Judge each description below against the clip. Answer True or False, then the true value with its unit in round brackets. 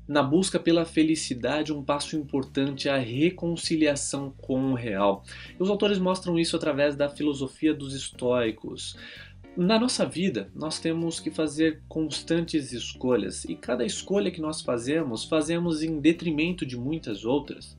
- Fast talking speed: False (150 wpm)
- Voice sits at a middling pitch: True (155 Hz)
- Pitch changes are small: False (3.5 semitones)